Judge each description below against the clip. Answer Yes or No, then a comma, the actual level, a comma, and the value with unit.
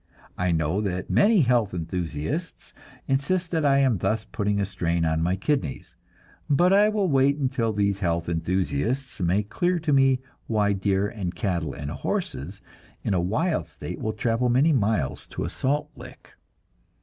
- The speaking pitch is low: Yes, low, 105 Hz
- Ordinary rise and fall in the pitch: No, wide, 7.4 semitones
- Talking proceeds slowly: No, average, 165 wpm